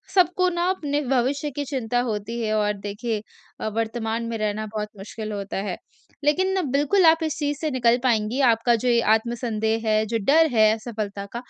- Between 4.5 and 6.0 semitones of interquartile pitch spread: Yes, average, 4.9 semitones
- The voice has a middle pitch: No, high, 235 Hz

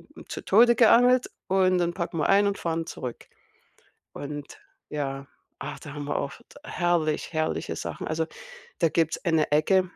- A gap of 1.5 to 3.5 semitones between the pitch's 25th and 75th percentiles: No, average, 4.3 semitones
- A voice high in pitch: No, medium, 165 Hz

